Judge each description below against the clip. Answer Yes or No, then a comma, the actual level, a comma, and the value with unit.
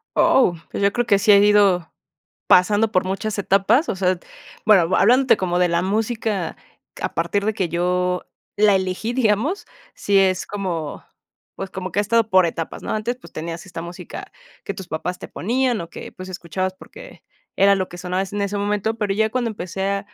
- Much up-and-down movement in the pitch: No, average, 2.9 semitones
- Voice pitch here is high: Yes, high, 195 Hz